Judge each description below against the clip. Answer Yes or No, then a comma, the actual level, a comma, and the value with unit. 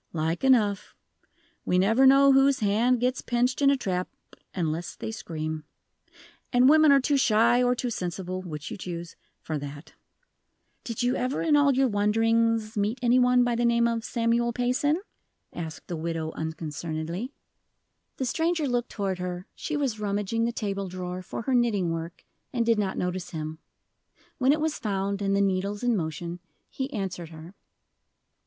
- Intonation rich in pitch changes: Yes, wide, 5.7 semitones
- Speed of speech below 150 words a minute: No, average, 170 wpm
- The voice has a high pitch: Yes, high, 215 Hz